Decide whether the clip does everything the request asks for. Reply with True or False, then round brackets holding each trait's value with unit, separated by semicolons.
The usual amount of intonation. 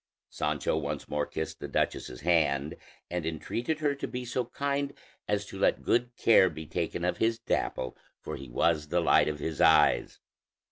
False (7.9 semitones)